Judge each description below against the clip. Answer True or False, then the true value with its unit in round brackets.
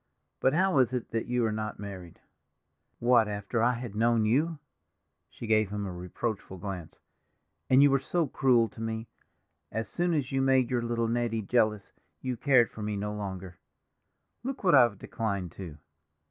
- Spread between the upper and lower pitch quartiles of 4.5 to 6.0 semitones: False (3.7 semitones)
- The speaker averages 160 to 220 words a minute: True (175 wpm)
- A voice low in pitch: True (115 Hz)